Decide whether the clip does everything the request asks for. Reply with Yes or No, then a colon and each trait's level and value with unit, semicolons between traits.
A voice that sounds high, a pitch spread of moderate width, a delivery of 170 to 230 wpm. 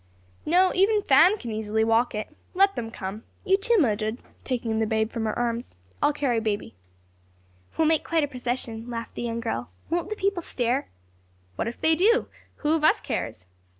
No: high, 245 Hz; wide, 6.8 semitones; average, 185 wpm